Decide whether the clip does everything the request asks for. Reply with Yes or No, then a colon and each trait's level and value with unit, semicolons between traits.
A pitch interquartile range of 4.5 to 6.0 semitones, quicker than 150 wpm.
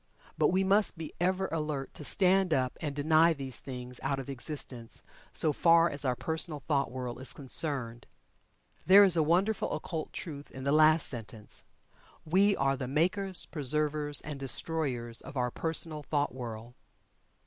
No: average, 3.9 semitones; average, 160 wpm